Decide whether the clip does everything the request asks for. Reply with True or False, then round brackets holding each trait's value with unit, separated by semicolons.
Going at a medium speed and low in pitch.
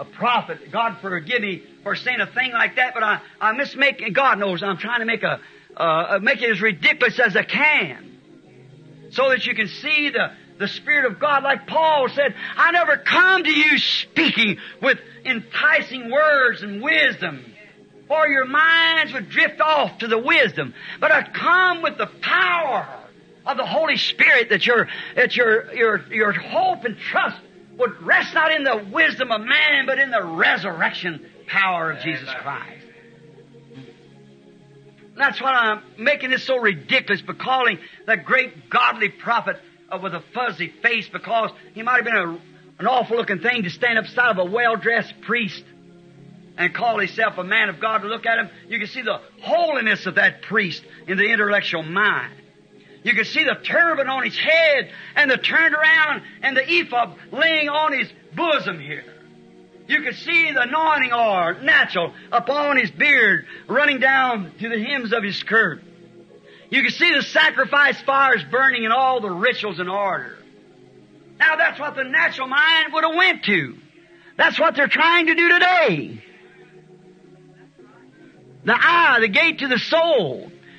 False (170 wpm; 250 Hz)